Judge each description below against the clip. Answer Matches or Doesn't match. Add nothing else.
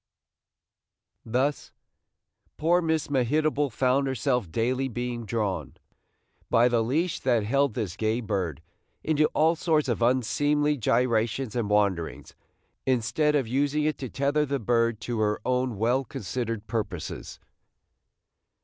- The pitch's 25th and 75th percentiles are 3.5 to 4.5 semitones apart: Matches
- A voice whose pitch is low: Matches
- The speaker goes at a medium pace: Doesn't match